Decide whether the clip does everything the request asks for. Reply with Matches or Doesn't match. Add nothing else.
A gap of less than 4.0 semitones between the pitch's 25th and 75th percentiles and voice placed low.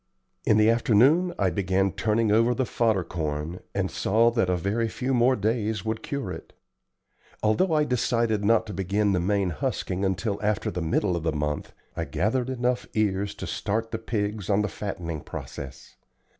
Matches